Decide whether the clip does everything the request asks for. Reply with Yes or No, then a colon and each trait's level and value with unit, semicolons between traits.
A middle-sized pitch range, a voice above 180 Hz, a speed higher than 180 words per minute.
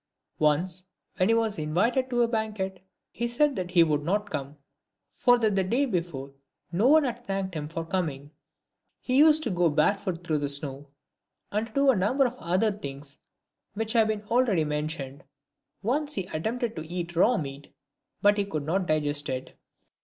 No: wide, 6.7 semitones; high, 190 Hz; average, 195 wpm